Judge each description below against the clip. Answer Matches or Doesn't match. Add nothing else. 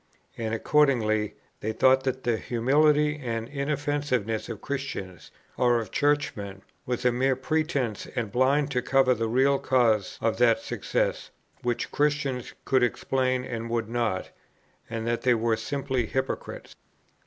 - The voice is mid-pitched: Doesn't match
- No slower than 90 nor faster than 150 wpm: Matches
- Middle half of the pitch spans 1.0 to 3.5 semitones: Matches